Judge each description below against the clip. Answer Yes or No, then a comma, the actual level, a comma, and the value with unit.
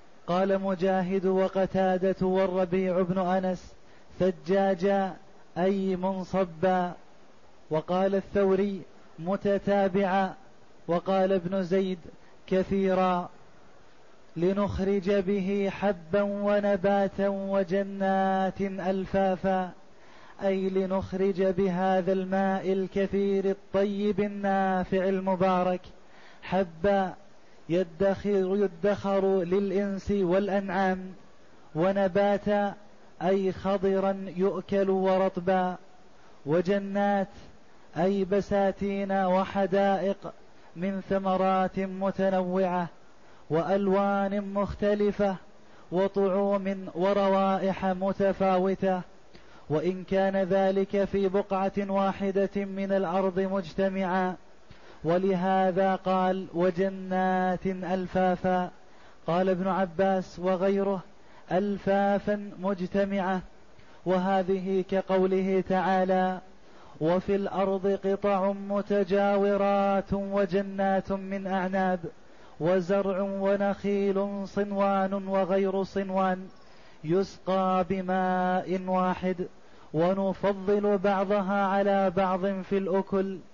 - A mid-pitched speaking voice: No, high, 195 Hz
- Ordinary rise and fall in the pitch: No, narrow, 0.9 semitones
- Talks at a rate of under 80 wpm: Yes, average, 70 wpm